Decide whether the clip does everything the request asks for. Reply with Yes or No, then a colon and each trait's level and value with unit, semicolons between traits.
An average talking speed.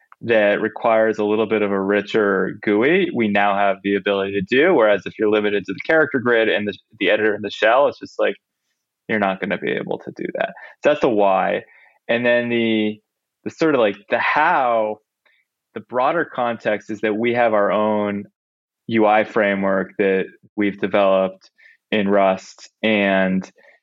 Yes: average, 185 wpm